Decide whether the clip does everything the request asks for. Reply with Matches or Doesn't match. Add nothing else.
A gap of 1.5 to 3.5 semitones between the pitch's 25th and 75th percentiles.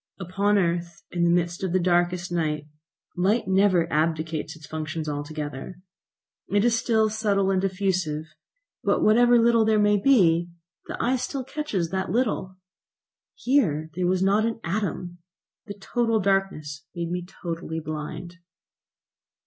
Doesn't match